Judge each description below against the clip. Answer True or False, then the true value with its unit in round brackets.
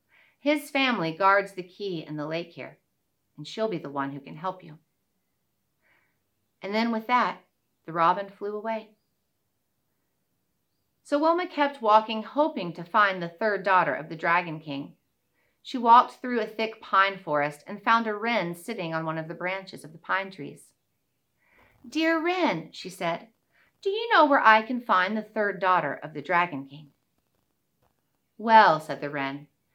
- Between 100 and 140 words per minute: False (165 wpm)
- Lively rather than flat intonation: True (5.7 semitones)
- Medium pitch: False (195 Hz)